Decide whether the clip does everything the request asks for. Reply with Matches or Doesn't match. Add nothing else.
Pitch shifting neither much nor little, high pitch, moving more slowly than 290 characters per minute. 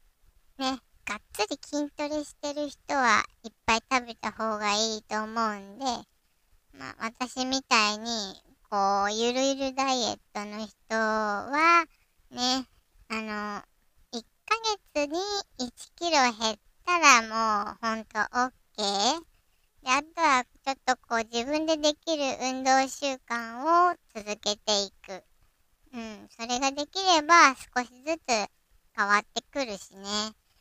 Matches